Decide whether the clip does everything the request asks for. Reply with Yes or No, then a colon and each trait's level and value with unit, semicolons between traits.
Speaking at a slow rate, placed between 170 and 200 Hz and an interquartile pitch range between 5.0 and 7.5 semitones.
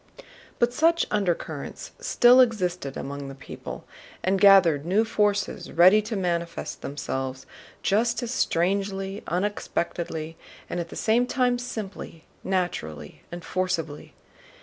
No: slow, 120 wpm; high, 190 Hz; average, 4.4 semitones